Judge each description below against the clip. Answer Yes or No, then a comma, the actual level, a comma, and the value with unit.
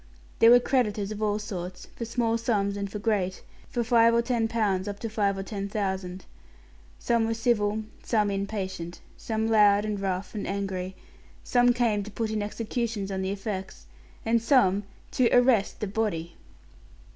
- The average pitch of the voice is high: Yes, high, 210 Hz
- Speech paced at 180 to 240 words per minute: No, average, 170 wpm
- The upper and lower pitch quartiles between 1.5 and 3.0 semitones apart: Yes, narrow, 2.6 semitones